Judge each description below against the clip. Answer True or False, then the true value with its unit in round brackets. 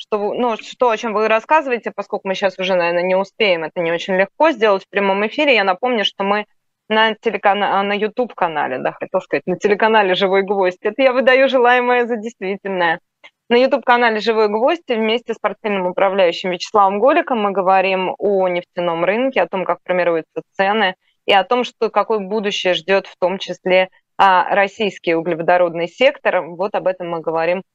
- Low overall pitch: False (200 Hz)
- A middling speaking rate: False (175 wpm)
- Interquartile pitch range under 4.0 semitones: True (3.5 semitones)